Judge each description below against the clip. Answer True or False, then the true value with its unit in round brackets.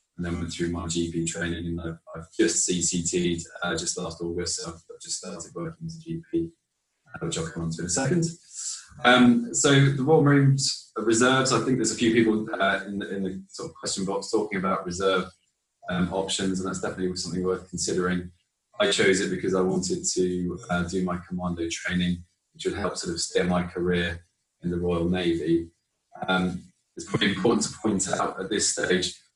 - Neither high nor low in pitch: False (90 Hz)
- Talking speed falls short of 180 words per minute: False (200 wpm)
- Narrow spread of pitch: False (4.8 semitones)